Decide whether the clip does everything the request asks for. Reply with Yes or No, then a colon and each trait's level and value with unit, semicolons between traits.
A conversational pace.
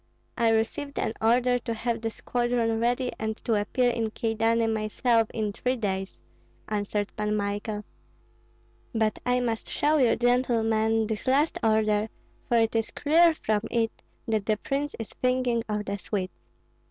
Yes: average, 155 wpm